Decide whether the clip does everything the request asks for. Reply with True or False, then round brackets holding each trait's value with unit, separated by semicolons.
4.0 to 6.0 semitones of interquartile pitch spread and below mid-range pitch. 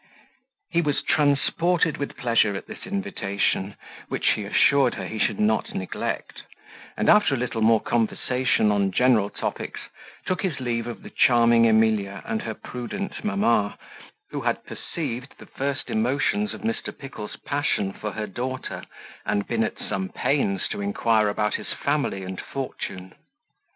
True (5.1 semitones; 115 Hz)